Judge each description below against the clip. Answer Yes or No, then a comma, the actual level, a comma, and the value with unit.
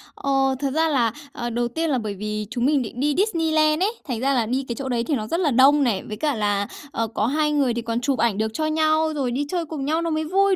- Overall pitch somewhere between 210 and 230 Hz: No, very high, 270 Hz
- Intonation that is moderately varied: Yes, average, 4.9 semitones